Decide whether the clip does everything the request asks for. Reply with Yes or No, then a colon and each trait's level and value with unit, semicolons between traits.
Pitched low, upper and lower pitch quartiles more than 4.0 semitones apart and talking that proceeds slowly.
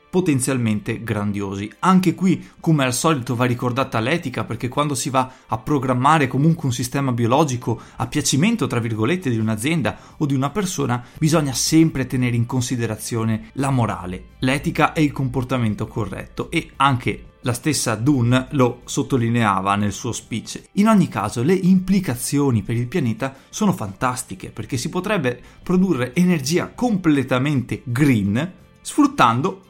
No: low, 130 Hz; average, 4.9 semitones; average, 140 wpm